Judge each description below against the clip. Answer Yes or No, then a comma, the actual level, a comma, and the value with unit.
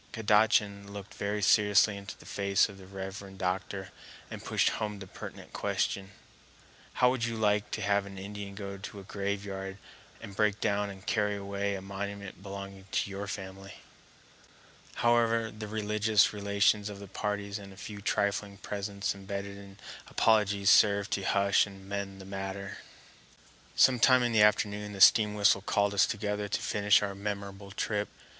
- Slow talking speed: No, average, 165 wpm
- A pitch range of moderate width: No, narrow, 0.9 semitones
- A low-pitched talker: Yes, low, 100 Hz